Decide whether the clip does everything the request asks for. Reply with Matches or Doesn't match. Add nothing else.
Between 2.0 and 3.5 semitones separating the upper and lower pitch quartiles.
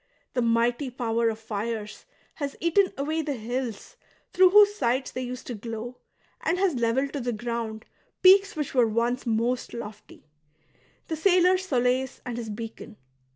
Doesn't match